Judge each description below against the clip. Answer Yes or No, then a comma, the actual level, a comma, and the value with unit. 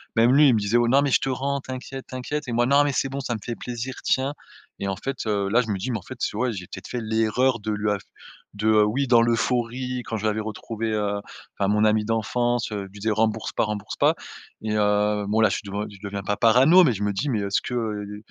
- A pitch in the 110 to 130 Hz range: Yes, low, 115 Hz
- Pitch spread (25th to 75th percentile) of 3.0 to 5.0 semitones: Yes, average, 3.4 semitones